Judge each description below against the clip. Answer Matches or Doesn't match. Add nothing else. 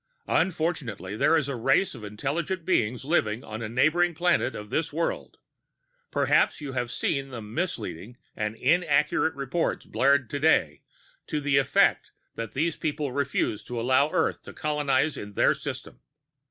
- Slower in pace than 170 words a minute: Matches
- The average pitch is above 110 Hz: Matches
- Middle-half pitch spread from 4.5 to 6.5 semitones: Matches